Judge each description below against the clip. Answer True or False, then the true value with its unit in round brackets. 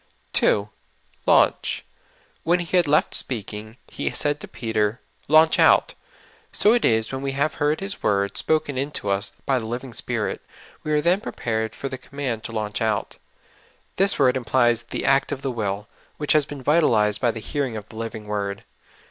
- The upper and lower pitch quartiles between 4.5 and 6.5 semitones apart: True (5.1 semitones)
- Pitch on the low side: True (125 Hz)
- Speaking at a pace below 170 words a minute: False (185 wpm)